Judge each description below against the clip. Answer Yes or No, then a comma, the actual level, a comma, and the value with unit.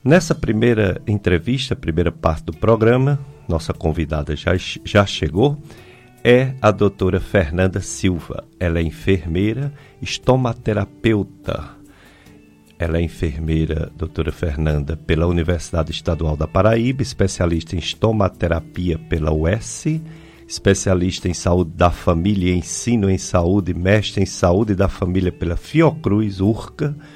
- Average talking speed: No, slow, 115 wpm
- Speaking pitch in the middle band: No, very low, 95 Hz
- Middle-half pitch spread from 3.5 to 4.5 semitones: No, average, 5.0 semitones